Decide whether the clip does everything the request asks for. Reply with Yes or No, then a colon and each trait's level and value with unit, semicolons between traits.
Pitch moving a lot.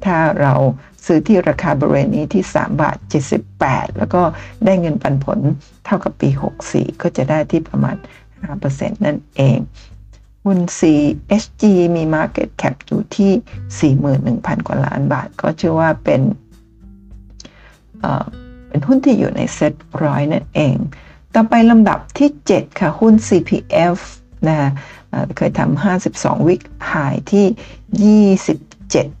Yes: wide, 6.7 semitones